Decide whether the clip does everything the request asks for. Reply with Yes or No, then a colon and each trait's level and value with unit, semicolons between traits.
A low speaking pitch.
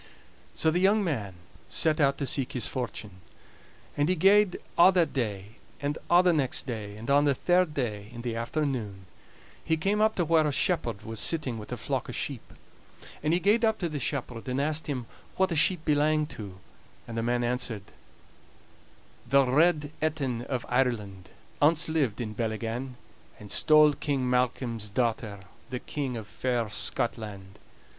Yes: low, 130 Hz